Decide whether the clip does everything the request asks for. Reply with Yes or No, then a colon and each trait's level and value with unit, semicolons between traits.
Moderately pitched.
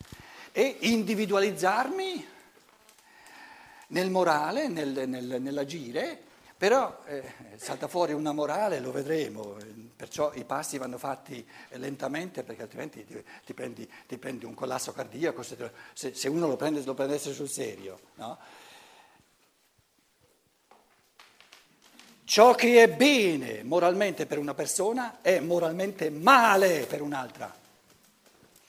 Yes: medium, 165 Hz